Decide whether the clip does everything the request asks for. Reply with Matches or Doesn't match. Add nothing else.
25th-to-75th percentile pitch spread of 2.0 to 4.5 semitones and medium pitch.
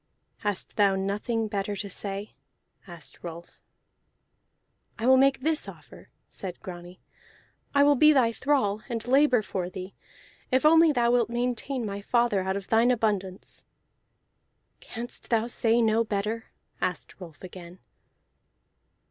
Doesn't match